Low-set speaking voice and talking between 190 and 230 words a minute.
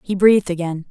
No: medium, 185 Hz; average, 200 wpm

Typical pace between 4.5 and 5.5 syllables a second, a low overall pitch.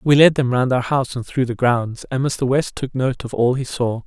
Yes: 5.0 syllables/s; low, 125 Hz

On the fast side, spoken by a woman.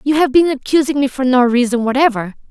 Yes: fast, 215 wpm; female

